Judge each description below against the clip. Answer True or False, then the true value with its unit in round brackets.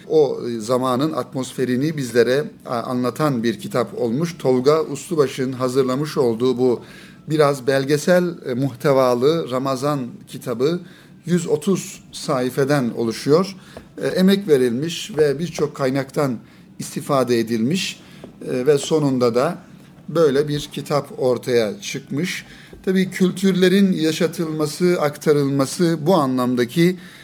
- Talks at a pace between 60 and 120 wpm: True (95 wpm)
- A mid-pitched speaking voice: True (150 Hz)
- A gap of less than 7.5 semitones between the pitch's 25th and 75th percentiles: True (5.3 semitones)